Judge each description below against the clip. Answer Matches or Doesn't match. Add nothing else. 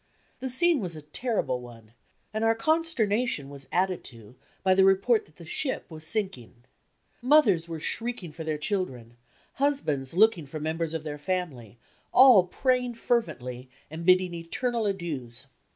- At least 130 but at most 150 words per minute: Doesn't match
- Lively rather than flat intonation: Matches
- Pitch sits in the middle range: Matches